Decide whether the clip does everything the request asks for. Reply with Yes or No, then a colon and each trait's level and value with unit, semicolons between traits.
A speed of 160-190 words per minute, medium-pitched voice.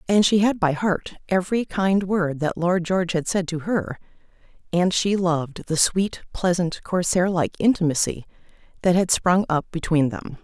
Yes: average, 165 wpm; medium, 175 Hz